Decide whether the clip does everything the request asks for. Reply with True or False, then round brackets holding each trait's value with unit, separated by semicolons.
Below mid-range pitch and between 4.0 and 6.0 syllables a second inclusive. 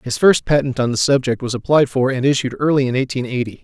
False (130 Hz; 6.2 syllables/s)